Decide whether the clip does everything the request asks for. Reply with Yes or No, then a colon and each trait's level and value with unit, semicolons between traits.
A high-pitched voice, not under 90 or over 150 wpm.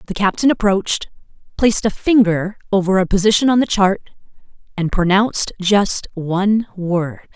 Yes: high, 195 Hz; average, 140 wpm